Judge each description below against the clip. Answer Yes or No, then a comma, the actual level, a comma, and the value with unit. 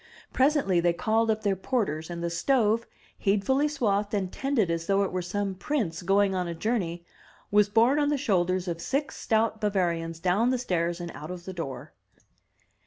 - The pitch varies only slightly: No, average, 4.7 semitones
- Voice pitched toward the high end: Yes, high, 195 Hz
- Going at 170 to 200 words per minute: Yes, average, 190 wpm